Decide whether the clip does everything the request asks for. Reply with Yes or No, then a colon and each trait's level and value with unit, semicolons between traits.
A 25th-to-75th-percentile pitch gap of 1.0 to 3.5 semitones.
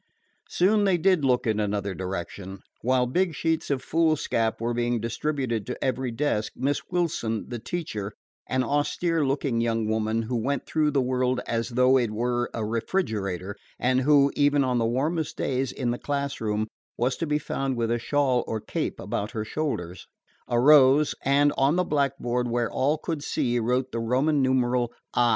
No: average, 3.9 semitones